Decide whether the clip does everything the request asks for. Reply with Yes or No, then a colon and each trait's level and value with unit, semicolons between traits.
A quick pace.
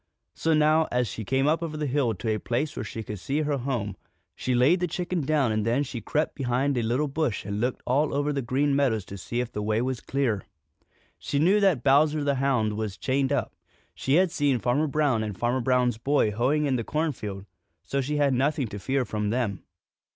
Yes: fast, 225 wpm